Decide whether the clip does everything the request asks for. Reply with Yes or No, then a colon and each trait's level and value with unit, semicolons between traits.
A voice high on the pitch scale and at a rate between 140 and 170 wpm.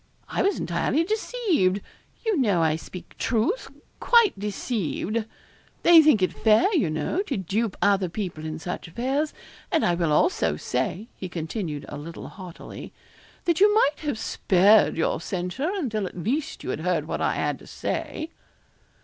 Yes: high, 215 Hz; average, 165 wpm